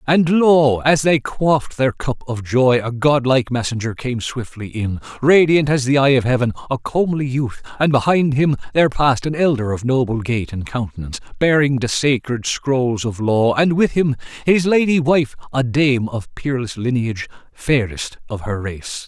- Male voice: Yes, male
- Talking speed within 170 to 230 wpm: Yes, average, 180 wpm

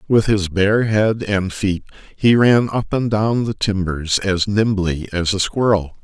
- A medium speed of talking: Yes, average, 180 wpm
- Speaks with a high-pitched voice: No, low, 100 Hz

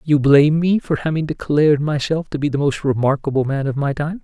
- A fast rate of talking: Yes, fast, 225 wpm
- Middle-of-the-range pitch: Yes, medium, 145 Hz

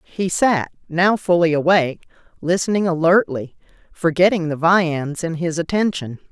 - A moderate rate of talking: No, slow, 125 wpm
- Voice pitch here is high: No, medium, 170 Hz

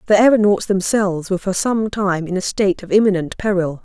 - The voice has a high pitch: Yes, high, 195 Hz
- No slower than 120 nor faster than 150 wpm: No, fast, 205 wpm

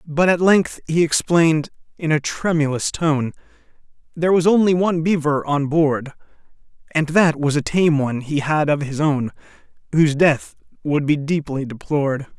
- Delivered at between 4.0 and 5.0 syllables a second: Yes, 4.9 syllables/s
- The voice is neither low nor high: Yes, medium, 155 Hz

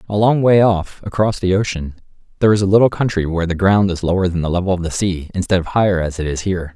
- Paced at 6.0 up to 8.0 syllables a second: Yes, 6.7 syllables/s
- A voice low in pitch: Yes, very low, 95 Hz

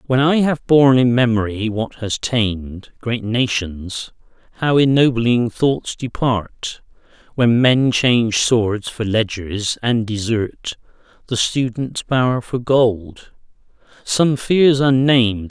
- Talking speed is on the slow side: Yes, slow, 115 wpm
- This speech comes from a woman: No, male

